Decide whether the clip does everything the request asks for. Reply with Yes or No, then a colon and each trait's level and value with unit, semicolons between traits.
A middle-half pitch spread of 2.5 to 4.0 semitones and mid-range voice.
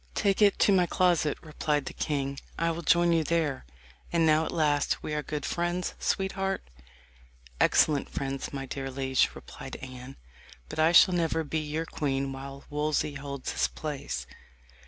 Yes: average, 3.4 semitones; medium, 150 Hz